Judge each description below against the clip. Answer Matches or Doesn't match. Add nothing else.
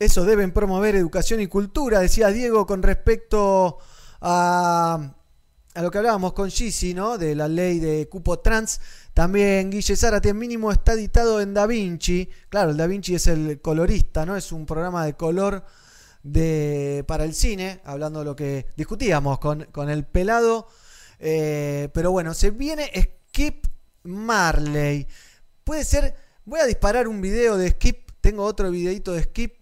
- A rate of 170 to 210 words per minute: Doesn't match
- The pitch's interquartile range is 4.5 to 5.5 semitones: Matches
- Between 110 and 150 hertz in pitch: Doesn't match